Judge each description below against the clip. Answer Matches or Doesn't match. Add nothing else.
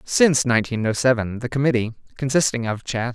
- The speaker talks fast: Doesn't match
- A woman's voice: Doesn't match